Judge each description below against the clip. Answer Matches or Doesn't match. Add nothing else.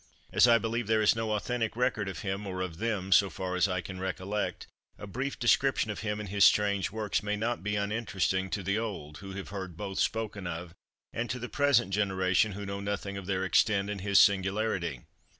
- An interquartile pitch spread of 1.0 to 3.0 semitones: Matches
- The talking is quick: Matches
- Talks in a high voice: Doesn't match